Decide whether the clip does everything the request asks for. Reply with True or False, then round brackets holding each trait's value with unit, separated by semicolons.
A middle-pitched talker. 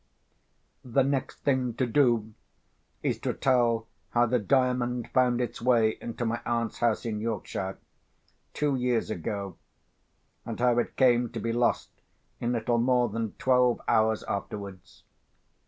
False (120 Hz)